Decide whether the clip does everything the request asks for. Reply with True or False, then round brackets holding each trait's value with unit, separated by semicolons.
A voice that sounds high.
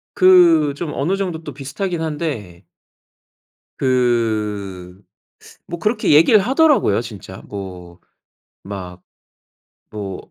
False (130 Hz)